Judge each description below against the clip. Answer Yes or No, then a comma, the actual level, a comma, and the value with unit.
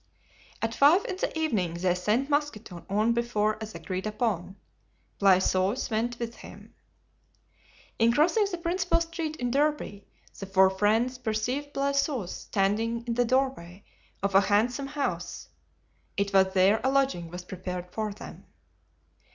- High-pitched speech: Yes, high, 225 Hz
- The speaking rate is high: No, average, 145 wpm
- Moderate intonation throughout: No, wide, 5.9 semitones